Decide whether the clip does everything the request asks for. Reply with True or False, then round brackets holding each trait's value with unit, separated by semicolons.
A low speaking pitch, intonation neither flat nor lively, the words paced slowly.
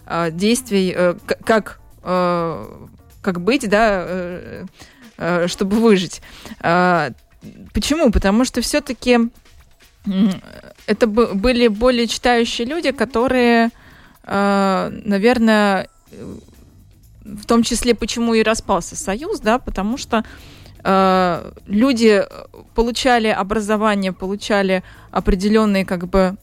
False (215 Hz; 3.7 semitones; 80 wpm)